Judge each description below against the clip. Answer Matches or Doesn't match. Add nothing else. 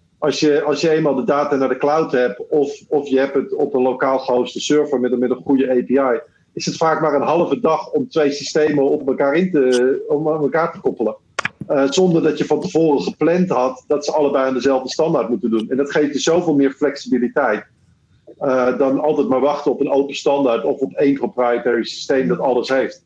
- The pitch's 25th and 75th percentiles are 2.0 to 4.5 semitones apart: Matches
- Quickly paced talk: Matches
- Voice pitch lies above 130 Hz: Matches